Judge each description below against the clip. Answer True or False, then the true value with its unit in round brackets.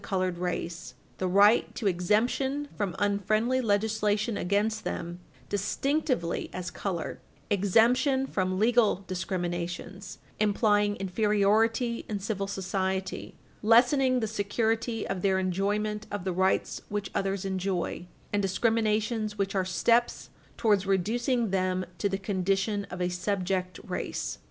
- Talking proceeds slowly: True (125 wpm)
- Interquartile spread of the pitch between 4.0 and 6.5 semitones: False (2.8 semitones)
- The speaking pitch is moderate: False (200 Hz)